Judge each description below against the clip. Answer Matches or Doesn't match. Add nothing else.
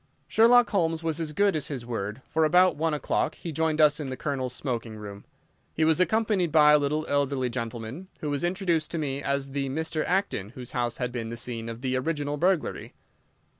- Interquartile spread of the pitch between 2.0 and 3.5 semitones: Doesn't match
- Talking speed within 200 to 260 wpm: Matches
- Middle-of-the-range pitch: Matches